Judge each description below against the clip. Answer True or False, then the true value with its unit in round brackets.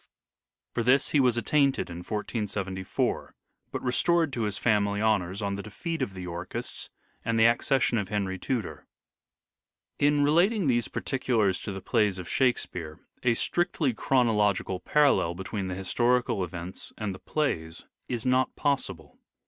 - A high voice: False (110 Hz)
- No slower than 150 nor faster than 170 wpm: True (155 wpm)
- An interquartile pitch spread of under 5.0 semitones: False (5.4 semitones)